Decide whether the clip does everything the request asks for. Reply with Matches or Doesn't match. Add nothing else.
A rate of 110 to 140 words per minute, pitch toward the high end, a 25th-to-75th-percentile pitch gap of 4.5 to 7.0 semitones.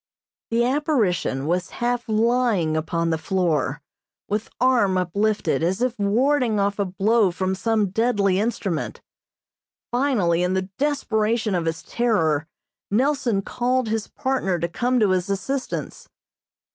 Matches